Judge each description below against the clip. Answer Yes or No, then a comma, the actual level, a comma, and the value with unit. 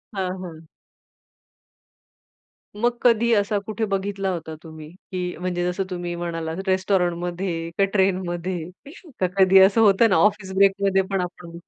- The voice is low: No, medium, 185 Hz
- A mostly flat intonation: Yes, narrow, 2.2 semitones